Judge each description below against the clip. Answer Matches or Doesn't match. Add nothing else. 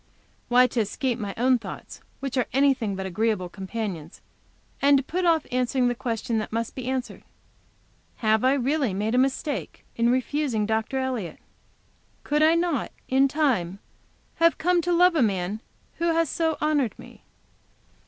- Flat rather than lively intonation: Doesn't match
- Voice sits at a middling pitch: Doesn't match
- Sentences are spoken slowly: Doesn't match